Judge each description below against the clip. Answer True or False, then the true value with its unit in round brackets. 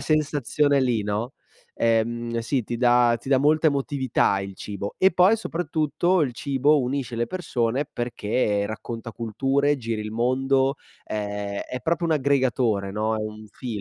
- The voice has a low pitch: True (125 Hz)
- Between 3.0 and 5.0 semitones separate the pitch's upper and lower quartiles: True (4.2 semitones)